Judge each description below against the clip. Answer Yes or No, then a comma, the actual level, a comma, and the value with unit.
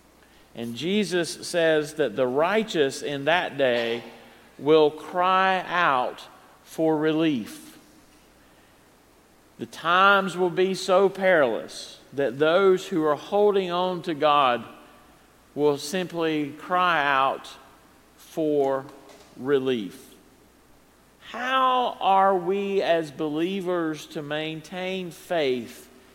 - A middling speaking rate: No, slow, 95 wpm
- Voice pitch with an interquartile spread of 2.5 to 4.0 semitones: No, average, 4.4 semitones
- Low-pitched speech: No, medium, 165 Hz